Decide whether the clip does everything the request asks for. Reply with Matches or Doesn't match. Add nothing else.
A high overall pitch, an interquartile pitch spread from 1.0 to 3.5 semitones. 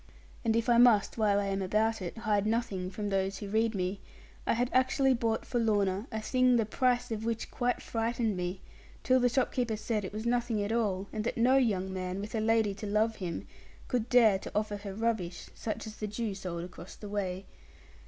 Matches